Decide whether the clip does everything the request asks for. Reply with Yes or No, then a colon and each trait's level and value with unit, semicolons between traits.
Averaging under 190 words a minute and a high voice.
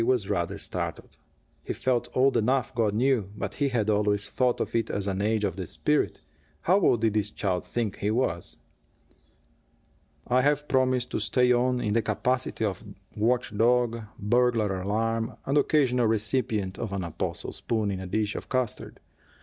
No: average, 175 wpm; low, 115 Hz